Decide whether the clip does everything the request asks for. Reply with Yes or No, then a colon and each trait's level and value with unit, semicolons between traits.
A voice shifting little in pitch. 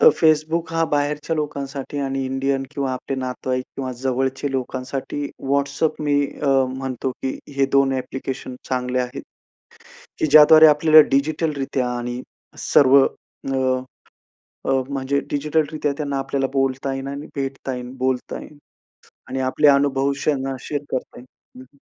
Yes: narrow, 1.7 semitones